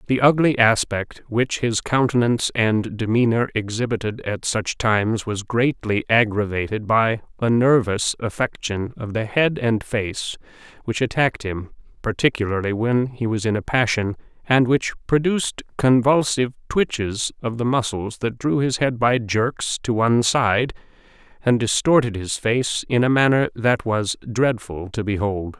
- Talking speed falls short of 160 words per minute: Yes, average, 150 wpm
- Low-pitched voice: Yes, low, 115 Hz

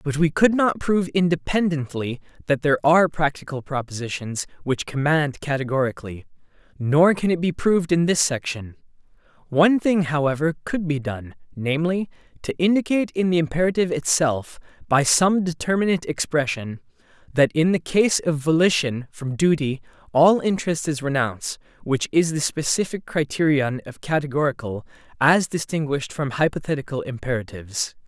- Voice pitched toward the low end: No, medium, 150 Hz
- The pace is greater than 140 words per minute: No, slow, 135 wpm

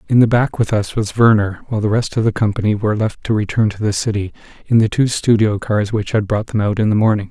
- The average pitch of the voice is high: No, low, 110 Hz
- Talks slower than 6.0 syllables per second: No, 6.2 syllables/s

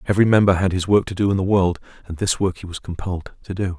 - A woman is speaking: No, male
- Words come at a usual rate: No, fast, 285 wpm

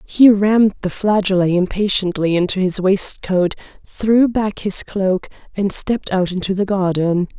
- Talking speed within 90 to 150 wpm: Yes, average, 145 wpm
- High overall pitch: Yes, high, 195 Hz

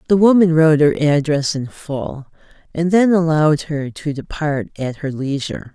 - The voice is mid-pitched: Yes, medium, 155 Hz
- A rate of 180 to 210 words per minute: No, average, 165 wpm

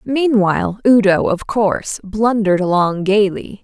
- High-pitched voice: Yes, high, 205 Hz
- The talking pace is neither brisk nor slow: No, slow, 115 wpm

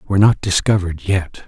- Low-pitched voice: Yes, very low, 95 Hz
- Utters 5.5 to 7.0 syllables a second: Yes, 6.2 syllables/s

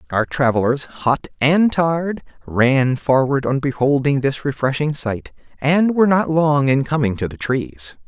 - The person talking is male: Yes, male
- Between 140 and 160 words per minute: Yes, average, 155 wpm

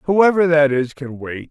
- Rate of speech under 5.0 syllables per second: Yes, 4.1 syllables/s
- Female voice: No, male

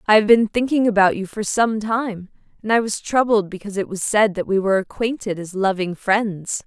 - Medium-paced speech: No, fast, 215 wpm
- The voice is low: No, high, 205 Hz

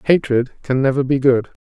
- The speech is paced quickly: No, average, 185 wpm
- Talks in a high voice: No, low, 130 Hz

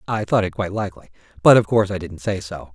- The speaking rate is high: Yes, fast, 260 wpm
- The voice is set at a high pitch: No, low, 100 Hz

